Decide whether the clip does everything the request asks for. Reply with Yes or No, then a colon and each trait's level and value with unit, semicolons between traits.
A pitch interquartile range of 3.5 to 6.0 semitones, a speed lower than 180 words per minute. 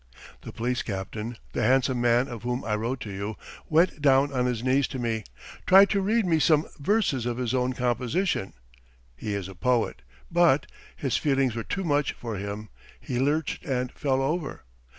No: average, 4.0 semitones; average, 185 wpm